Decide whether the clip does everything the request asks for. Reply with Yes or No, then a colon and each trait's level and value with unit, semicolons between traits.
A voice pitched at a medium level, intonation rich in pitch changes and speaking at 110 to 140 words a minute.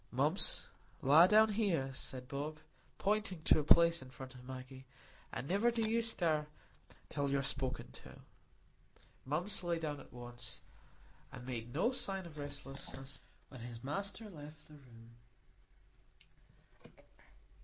Yes: medium, 145 Hz; wide, 5.8 semitones; slow, 135 wpm